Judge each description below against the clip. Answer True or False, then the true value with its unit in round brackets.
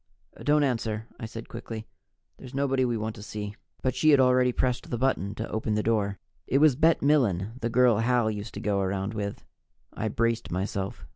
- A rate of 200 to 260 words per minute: True (205 wpm)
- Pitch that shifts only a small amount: False (3.4 semitones)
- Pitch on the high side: False (115 Hz)